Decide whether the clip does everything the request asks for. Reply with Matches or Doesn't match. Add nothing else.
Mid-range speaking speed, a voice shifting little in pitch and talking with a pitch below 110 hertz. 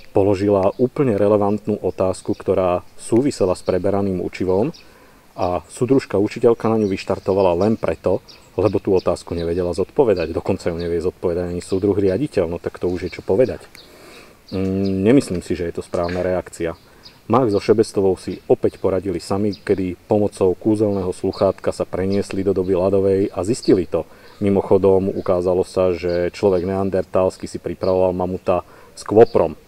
Matches